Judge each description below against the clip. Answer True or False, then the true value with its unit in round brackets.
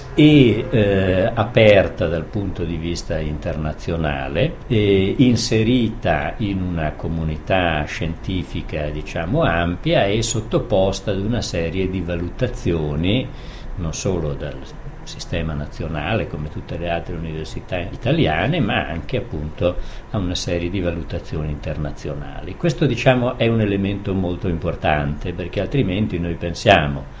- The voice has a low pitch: True (90 Hz)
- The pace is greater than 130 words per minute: False (115 wpm)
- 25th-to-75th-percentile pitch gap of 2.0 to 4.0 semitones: False (4.7 semitones)